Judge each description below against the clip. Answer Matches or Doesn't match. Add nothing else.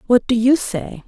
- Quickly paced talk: Matches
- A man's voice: Doesn't match